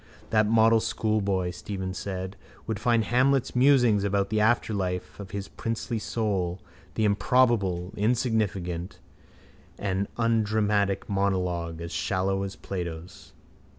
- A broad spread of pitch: No, average, 3.2 semitones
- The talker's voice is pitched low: Yes, low, 100 Hz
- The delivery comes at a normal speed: No, slow, 115 wpm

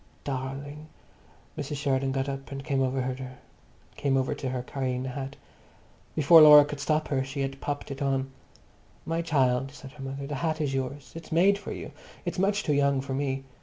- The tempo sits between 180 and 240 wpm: Yes, average, 185 wpm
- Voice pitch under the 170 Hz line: Yes, medium, 140 Hz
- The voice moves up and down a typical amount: No, narrow, 1.8 semitones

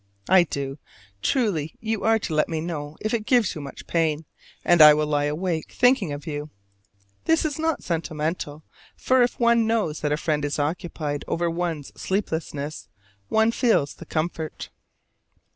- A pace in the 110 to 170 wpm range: Yes, average, 165 wpm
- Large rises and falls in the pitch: Yes, wide, 6.4 semitones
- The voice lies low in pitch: No, medium, 165 Hz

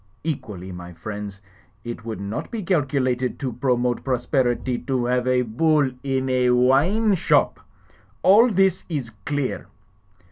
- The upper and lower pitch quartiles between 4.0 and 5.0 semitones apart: No, average, 3.5 semitones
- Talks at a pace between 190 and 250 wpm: No, average, 140 wpm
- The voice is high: No, low, 130 Hz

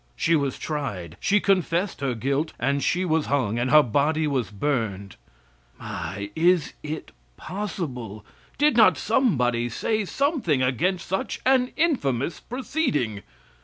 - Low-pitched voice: No, medium, 150 Hz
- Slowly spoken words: Yes, slow, 130 wpm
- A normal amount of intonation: No, wide, 7.8 semitones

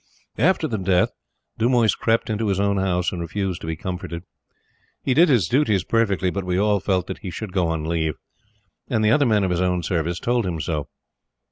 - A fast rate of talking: Yes, fast, 210 wpm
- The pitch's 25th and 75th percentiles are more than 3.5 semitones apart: Yes, average, 3.9 semitones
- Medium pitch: No, very low, 95 Hz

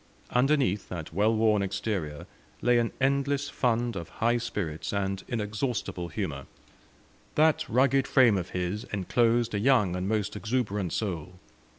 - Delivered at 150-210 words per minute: No, slow, 135 wpm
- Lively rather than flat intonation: No, average, 4.1 semitones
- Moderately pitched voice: No, low, 110 Hz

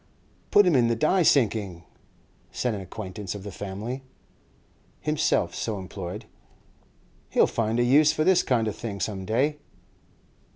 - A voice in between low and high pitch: No, low, 110 Hz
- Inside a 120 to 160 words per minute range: Yes, average, 150 wpm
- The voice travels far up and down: Yes, wide, 5.7 semitones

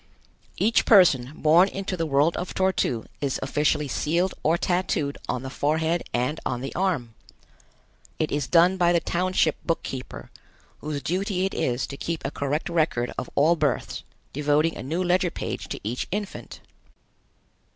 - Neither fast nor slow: Yes, average, 165 wpm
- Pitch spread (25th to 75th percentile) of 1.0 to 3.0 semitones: No, average, 4.3 semitones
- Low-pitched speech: No, medium, 160 Hz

